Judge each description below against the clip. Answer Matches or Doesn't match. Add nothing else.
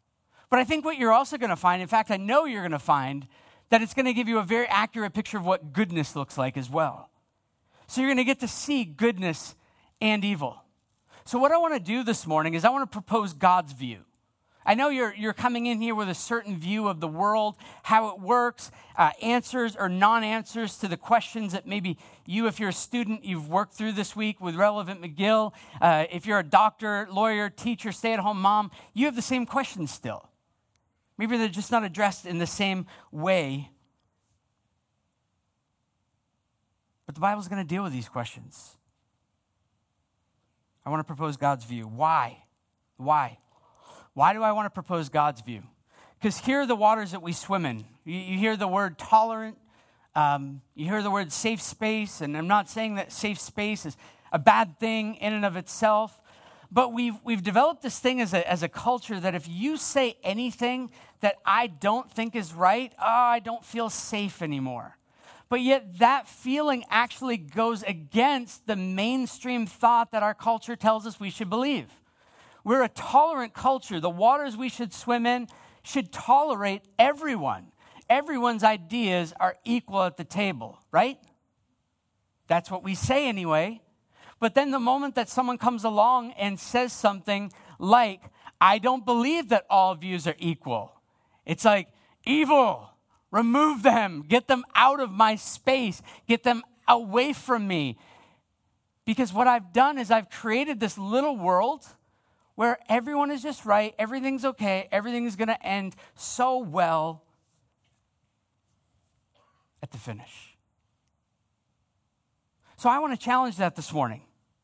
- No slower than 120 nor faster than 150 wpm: Doesn't match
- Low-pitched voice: Doesn't match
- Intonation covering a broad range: Matches